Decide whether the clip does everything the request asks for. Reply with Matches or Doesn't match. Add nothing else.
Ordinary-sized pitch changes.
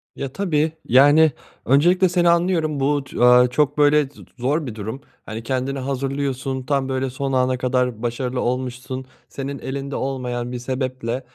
Doesn't match